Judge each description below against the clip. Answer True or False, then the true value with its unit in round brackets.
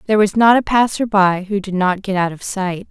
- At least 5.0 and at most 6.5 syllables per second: True (5.5 syllables/s)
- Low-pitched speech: False (200 Hz)